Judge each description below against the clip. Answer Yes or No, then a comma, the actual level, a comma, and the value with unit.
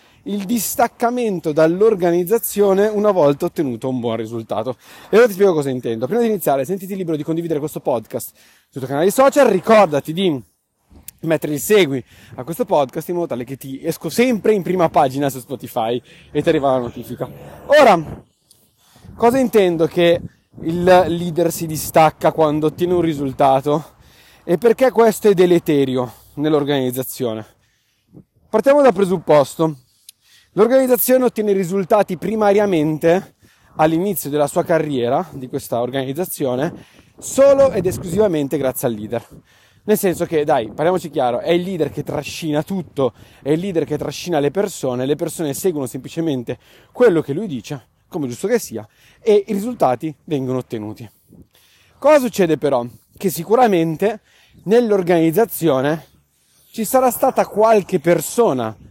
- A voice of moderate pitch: Yes, medium, 165 Hz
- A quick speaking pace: No, average, 140 wpm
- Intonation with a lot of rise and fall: Yes, wide, 6.6 semitones